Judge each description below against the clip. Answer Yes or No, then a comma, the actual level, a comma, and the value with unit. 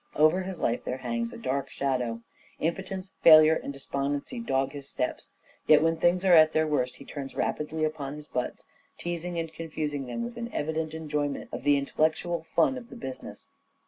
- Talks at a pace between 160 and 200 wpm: Yes, average, 185 wpm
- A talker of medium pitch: Yes, medium, 155 Hz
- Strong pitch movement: No, average, 3.2 semitones